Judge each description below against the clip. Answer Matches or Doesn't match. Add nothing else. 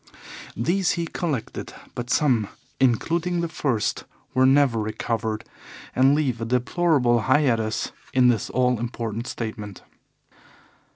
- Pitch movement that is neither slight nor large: Matches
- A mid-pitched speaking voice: Doesn't match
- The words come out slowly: Matches